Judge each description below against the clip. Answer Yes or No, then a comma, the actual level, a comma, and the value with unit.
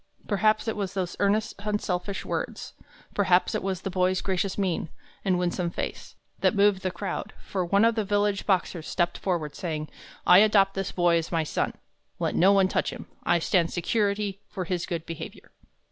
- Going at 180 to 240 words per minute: Yes, average, 185 wpm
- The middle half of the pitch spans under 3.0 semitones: Yes, narrow, 2.4 semitones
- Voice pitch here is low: No, high, 190 Hz